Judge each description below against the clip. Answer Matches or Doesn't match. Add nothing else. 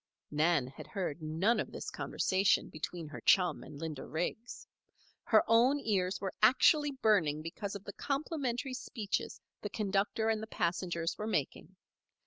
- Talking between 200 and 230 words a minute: Doesn't match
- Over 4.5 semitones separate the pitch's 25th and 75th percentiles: Matches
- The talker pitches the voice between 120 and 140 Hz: Doesn't match